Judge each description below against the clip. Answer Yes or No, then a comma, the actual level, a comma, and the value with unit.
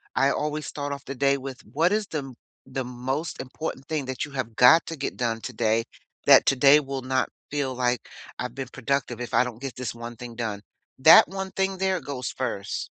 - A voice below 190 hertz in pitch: Yes, low, 135 Hz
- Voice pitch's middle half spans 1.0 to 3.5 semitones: Yes, average, 2.8 semitones